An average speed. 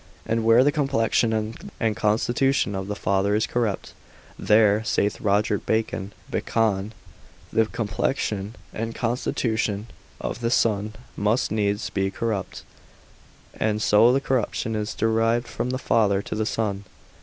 No: slow, 130 wpm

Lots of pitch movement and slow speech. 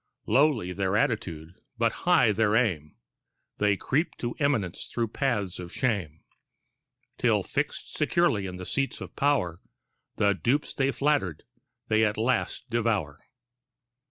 Yes: wide, 6.2 semitones; slow, 130 wpm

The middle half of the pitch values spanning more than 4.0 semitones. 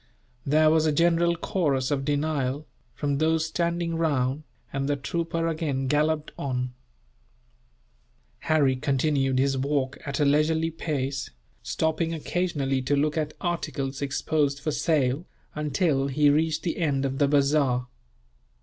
No: average, 2.7 semitones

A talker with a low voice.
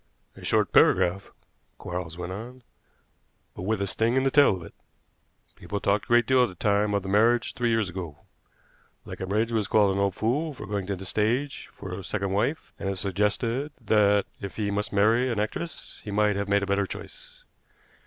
Yes: low, 105 Hz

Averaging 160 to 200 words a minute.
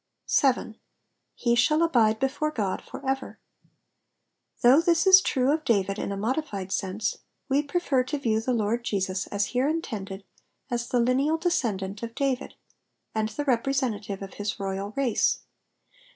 No: average, 150 wpm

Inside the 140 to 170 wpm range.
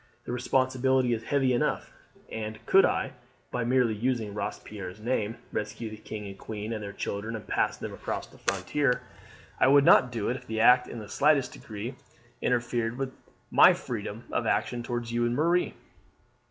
No: average, 180 wpm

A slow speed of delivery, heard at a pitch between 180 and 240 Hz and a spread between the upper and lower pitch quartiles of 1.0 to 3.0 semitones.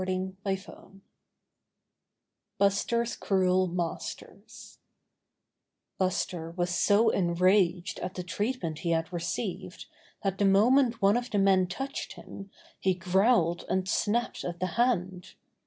Yes: slow, 125 wpm; high, 190 Hz; narrow, 2.5 semitones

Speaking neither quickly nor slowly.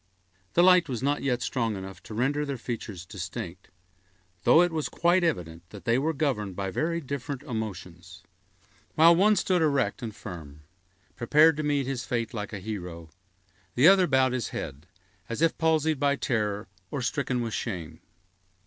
Yes: average, 165 wpm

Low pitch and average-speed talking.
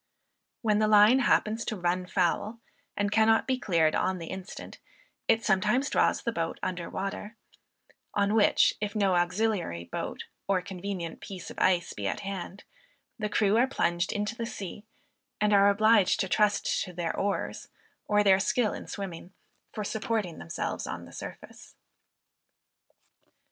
No: high, 200 Hz; average, 155 wpm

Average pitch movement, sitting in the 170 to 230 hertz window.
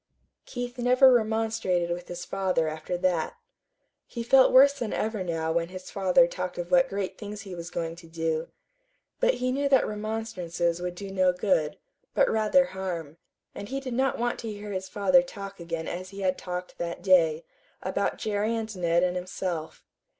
Yes: average, 4.2 semitones; high, 190 Hz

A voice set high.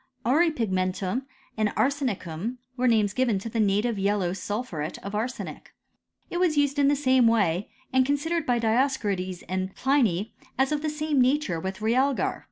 Yes: high, 235 Hz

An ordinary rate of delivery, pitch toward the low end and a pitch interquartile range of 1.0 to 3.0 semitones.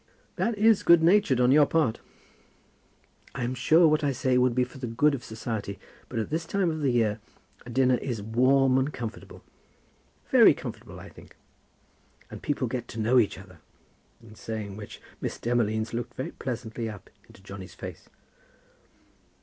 No: average, 170 wpm; low, 125 Hz; average, 4.0 semitones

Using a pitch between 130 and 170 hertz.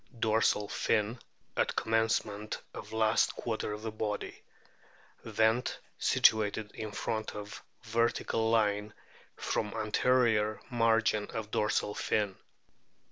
No: low, 110 Hz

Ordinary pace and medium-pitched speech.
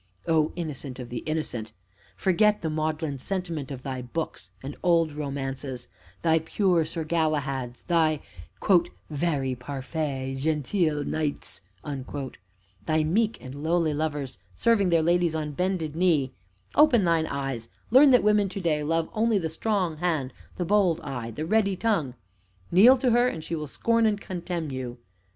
Yes: average, 150 wpm; medium, 160 Hz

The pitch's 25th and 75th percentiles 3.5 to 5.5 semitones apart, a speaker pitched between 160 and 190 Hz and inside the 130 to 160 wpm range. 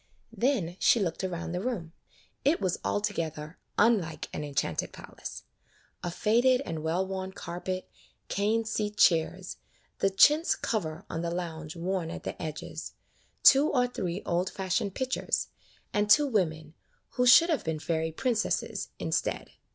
Yes: average, 5.2 semitones; medium, 185 Hz; average, 150 wpm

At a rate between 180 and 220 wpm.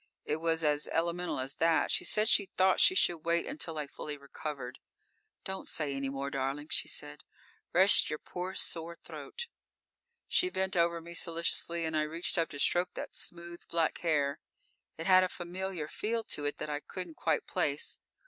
Yes: average, 185 wpm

